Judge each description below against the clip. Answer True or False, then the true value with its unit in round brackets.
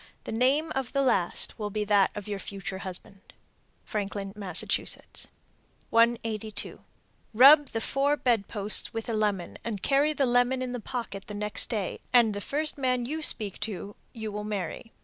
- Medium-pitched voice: False (220 Hz)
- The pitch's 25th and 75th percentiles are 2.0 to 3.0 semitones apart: False (3.8 semitones)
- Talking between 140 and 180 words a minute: True (170 wpm)